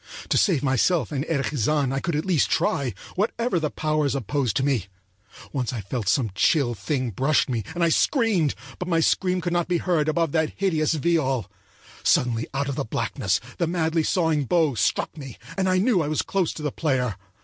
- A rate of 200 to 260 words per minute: Yes, fast, 205 wpm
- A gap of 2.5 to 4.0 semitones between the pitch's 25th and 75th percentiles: No, average, 4.5 semitones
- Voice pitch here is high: No, medium, 150 Hz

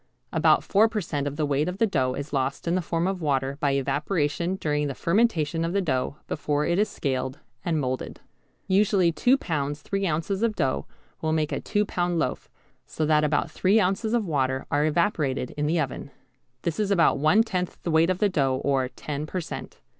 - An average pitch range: Yes, average, 4.7 semitones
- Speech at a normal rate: No, fast, 210 wpm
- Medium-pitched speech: Yes, medium, 160 Hz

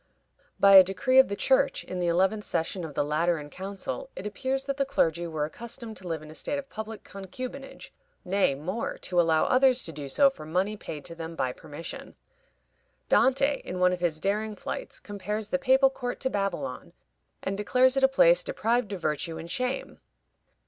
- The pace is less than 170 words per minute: No, average, 195 wpm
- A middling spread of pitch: No, wide, 7.5 semitones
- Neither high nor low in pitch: No, high, 200 Hz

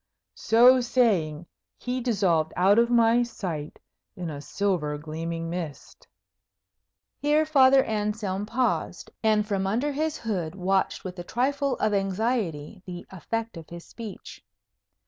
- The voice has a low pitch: No, high, 205 Hz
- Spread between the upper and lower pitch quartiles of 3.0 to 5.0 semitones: No, wide, 5.5 semitones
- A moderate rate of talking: No, slow, 130 wpm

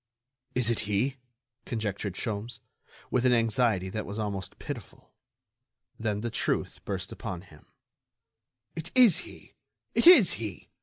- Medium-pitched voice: No, low, 110 Hz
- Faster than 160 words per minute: No, slow, 135 wpm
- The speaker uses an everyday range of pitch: Yes, average, 3.6 semitones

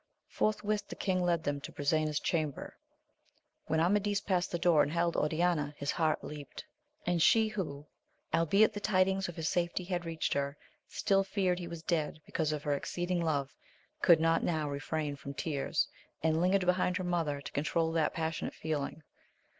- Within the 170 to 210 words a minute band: Yes, average, 175 wpm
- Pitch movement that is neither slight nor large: Yes, average, 3.1 semitones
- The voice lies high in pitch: No, medium, 165 Hz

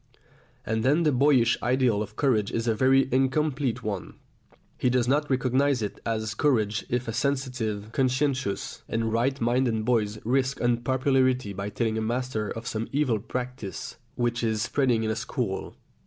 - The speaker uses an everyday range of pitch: Yes, average, 3.0 semitones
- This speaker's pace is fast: No, average, 160 wpm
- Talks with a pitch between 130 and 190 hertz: No, low, 120 Hz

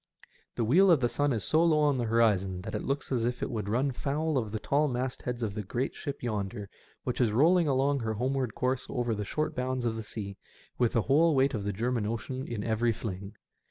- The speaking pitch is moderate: No, low, 120 Hz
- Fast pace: Yes, fast, 235 wpm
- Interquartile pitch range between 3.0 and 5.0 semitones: Yes, average, 3.9 semitones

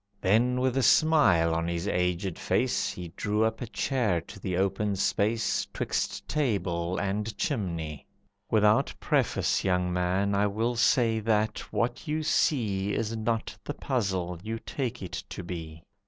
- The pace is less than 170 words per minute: Yes, average, 155 wpm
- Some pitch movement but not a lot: Yes, average, 4.2 semitones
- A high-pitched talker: No, low, 105 Hz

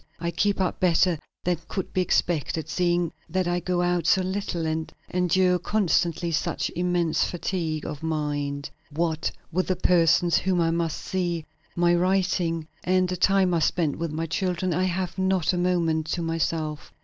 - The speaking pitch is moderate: Yes, medium, 175 Hz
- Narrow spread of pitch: Yes, narrow, 2.0 semitones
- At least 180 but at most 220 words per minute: No, average, 170 wpm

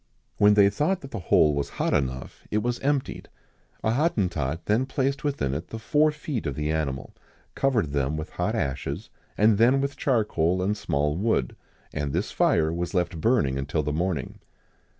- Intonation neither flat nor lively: No, wide, 8.4 semitones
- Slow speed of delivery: No, average, 180 wpm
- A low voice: Yes, very low, 95 Hz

